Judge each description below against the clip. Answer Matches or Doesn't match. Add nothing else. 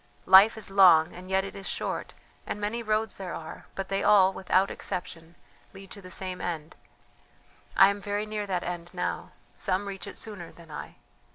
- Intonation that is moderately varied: Doesn't match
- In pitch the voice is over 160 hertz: Matches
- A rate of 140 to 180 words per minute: Doesn't match